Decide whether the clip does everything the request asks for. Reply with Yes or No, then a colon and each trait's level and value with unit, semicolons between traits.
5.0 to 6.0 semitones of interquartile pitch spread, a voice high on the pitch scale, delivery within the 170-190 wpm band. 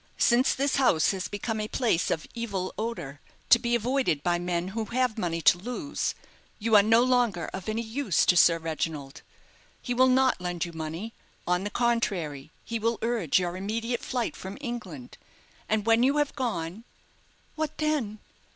Yes: wide, 5.5 semitones; high, 220 Hz; average, 180 wpm